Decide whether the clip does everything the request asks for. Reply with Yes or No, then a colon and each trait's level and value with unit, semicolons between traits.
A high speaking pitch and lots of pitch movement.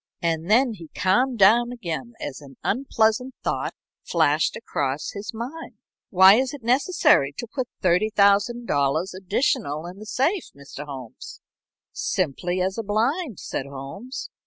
Yes: high, 200 Hz; wide, 6.9 semitones